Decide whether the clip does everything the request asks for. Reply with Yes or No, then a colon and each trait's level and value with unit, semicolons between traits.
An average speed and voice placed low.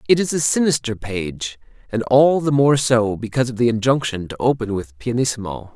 Yes: average, 190 wpm; low, 120 Hz